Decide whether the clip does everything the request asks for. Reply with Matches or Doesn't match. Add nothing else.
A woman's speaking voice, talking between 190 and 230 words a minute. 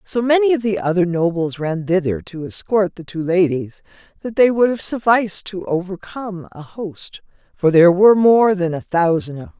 Matches